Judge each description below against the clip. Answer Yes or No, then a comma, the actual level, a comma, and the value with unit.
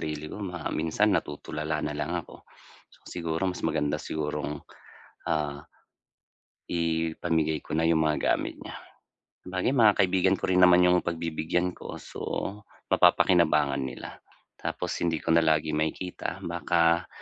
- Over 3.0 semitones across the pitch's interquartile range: No, narrow, 2.5 semitones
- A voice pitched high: No, very low, 80 Hz